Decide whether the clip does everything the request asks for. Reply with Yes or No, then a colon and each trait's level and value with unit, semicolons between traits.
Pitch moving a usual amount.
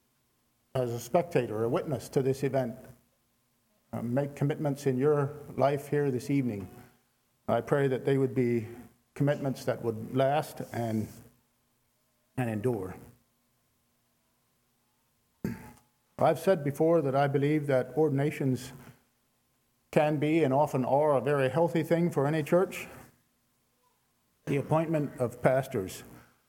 Yes: average, 3.5 semitones